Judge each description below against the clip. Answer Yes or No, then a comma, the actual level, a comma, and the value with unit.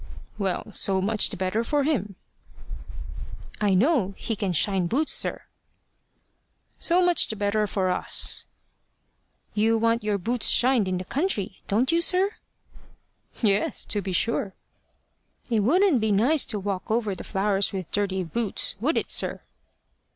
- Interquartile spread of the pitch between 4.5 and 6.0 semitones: No, average, 3.9 semitones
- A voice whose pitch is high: Yes, high, 210 Hz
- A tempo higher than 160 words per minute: No, average, 150 wpm